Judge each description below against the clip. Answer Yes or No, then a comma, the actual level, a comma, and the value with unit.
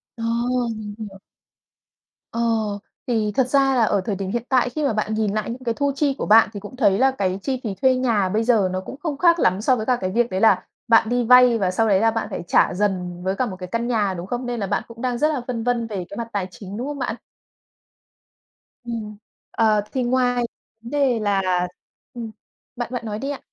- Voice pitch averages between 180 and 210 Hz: No, high, 225 Hz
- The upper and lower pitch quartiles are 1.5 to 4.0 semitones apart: Yes, average, 3.6 semitones